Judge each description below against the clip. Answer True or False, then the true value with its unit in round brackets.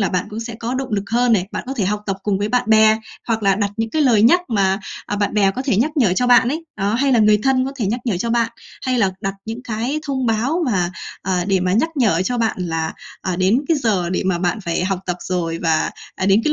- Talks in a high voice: True (215 Hz)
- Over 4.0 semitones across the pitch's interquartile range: True (4.4 semitones)